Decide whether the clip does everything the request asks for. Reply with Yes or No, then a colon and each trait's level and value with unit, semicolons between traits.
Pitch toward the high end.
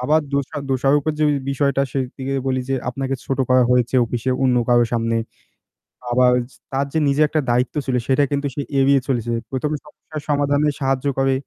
No: low, 135 Hz